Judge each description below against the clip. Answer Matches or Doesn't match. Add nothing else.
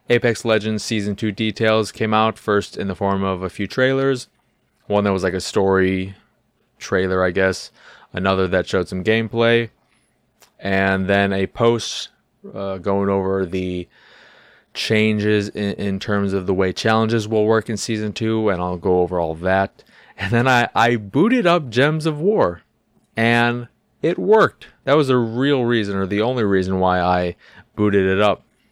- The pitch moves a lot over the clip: Doesn't match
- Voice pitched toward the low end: Matches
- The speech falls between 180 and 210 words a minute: Doesn't match